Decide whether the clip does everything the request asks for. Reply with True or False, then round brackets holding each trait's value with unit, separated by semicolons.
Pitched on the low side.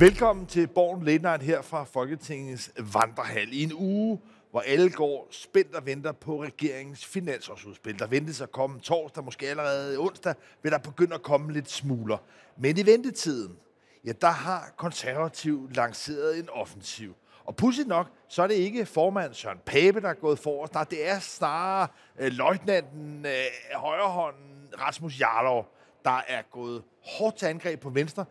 False (150 Hz)